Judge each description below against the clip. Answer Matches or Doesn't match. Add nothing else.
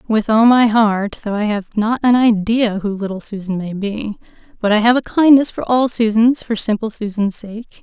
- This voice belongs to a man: Doesn't match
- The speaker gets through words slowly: Doesn't match